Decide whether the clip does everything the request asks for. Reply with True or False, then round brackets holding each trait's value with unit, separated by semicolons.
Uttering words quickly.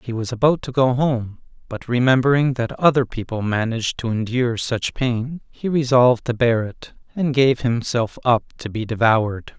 False (175 wpm)